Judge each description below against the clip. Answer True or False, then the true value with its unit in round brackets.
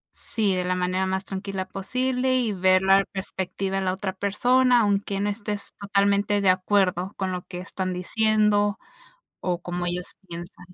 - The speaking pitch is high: True (195 Hz)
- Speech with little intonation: True (1.9 semitones)